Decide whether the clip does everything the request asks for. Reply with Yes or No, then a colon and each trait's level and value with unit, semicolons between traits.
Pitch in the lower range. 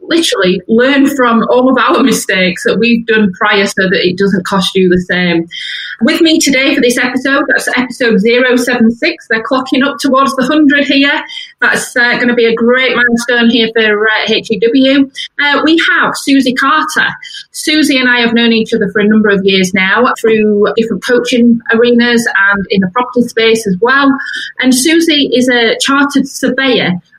No: high, 240 Hz